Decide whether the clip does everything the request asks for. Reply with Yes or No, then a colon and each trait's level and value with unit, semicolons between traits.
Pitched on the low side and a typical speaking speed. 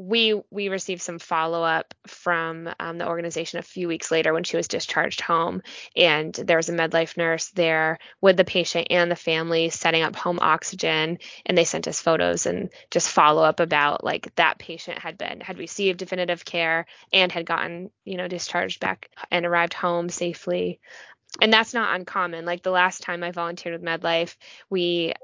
No: medium, 170 Hz; average, 185 wpm